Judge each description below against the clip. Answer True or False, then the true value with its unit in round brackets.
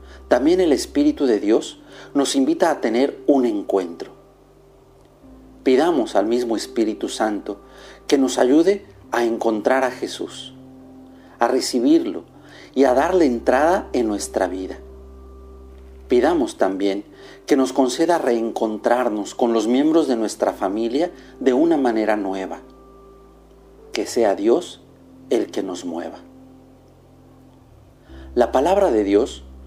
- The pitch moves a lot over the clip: True (7.1 semitones)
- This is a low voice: True (120 Hz)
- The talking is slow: True (120 wpm)